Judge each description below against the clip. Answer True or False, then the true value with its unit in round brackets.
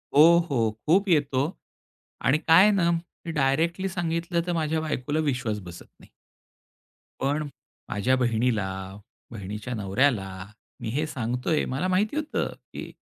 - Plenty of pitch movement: True (6.1 semitones)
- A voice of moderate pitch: True (145 Hz)